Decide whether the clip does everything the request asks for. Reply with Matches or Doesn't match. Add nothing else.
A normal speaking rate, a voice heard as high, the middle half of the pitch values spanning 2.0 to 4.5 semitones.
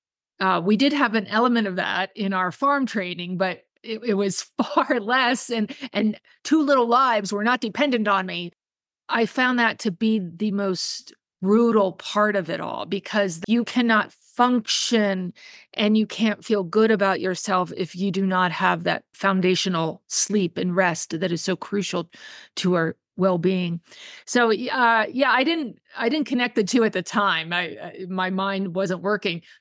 Matches